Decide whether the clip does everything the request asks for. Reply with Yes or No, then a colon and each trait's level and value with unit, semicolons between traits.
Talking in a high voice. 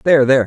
No: low, 135 Hz